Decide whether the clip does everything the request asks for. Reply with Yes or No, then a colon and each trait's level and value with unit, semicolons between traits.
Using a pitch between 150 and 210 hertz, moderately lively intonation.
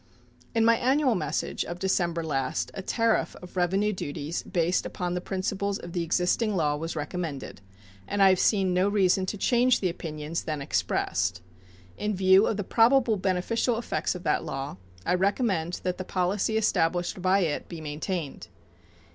Yes: medium, 185 Hz; average, 3.5 semitones